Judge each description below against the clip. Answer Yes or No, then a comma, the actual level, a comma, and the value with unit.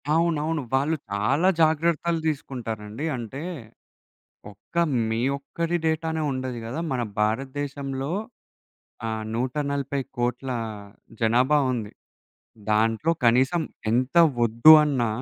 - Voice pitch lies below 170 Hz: Yes, low, 135 Hz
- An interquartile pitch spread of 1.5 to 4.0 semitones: No, average, 4.8 semitones